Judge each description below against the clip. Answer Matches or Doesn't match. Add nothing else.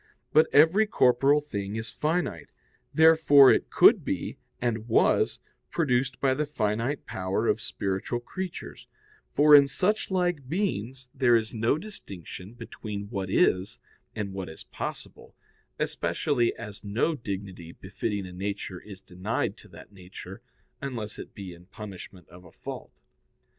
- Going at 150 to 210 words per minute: Doesn't match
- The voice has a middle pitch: Doesn't match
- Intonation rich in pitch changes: Matches